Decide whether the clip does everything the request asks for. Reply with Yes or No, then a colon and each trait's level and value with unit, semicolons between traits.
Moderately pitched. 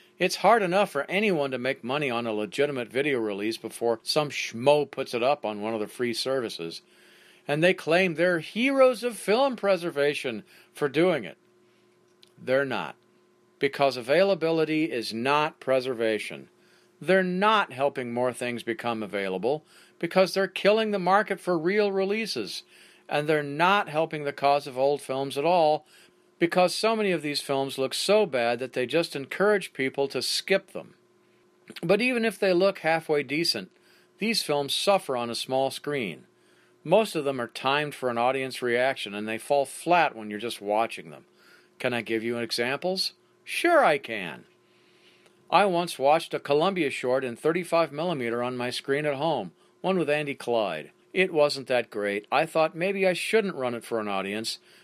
Yes: medium, 145 Hz